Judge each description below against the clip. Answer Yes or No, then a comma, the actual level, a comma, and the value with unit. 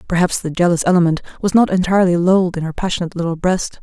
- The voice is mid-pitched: Yes, medium, 175 Hz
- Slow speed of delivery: No, fast, 205 wpm